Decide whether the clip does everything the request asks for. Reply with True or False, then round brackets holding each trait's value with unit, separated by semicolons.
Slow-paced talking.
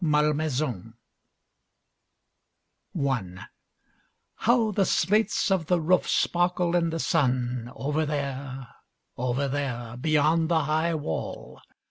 True (100 wpm)